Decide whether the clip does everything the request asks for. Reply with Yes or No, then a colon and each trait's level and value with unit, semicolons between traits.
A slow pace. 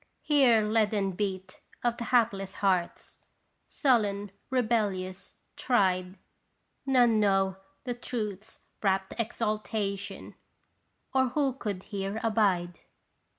Yes: slow, 95 wpm